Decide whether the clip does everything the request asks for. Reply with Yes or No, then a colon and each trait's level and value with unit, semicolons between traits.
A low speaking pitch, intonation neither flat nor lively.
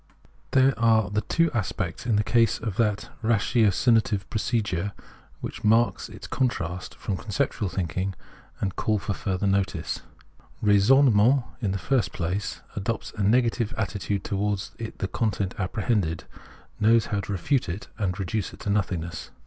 Yes: low, 105 Hz; average, 3.0 semitones